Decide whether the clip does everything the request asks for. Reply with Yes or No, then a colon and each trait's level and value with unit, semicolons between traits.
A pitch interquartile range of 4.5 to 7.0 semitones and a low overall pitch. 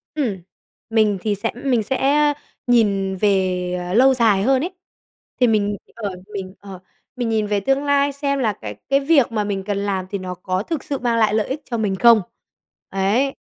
No: average, 5.1 semitones; high, 215 Hz